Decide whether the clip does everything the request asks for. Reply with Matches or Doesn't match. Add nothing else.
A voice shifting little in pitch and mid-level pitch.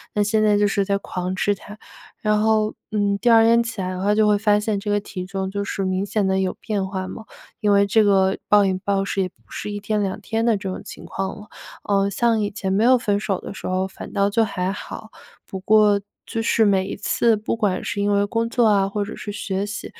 Doesn't match